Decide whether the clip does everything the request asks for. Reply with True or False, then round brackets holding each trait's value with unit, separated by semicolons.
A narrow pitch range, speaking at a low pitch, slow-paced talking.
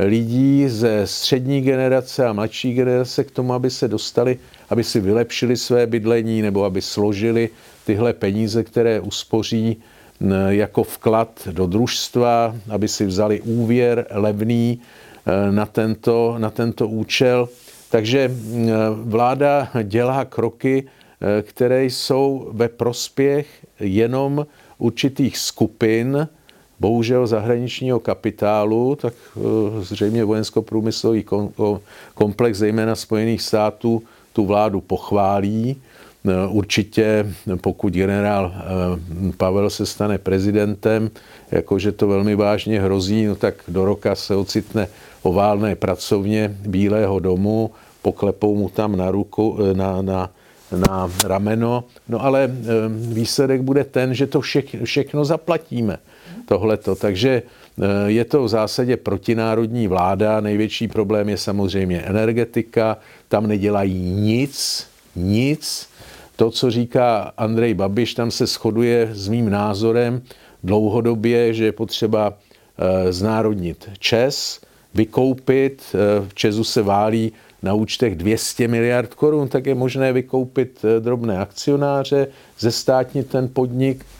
False (3.0 semitones; 110 Hz; 110 wpm)